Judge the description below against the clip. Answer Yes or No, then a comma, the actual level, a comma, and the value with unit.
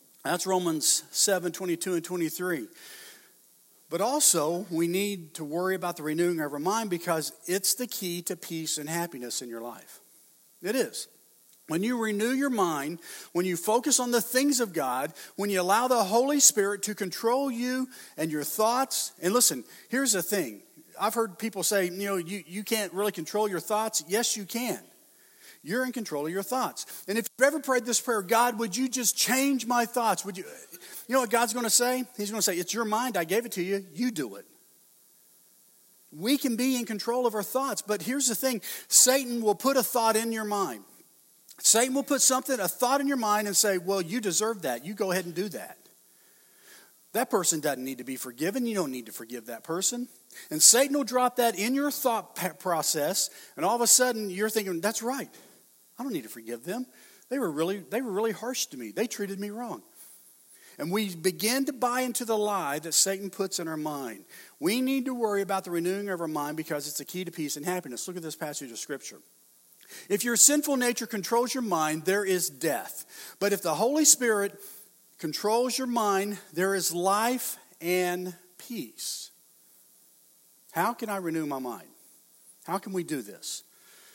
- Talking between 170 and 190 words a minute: No, fast, 205 wpm